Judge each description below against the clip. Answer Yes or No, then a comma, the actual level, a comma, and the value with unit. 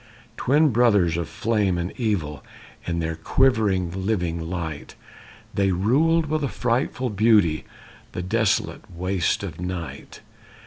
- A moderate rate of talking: No, slow, 125 wpm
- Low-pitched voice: Yes, very low, 95 Hz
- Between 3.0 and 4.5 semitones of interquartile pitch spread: No, average, 5.3 semitones